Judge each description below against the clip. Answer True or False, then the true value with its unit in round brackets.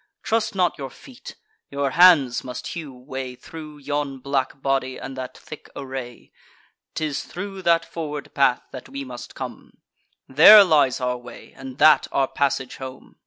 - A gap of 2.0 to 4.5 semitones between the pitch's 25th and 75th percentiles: True (3.2 semitones)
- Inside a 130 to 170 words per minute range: True (160 wpm)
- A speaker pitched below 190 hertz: True (140 Hz)